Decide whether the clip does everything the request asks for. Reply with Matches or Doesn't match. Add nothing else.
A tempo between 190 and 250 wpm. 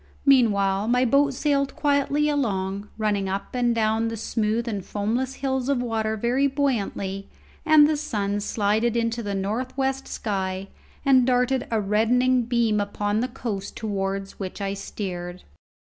Doesn't match